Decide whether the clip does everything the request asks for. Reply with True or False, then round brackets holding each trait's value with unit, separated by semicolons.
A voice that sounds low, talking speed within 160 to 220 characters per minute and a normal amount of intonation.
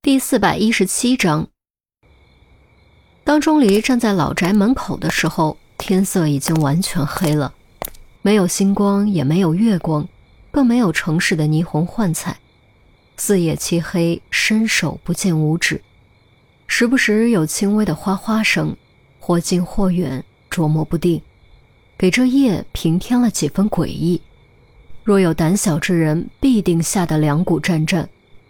False (180 Hz; 205 characters per minute; 4.5 semitones)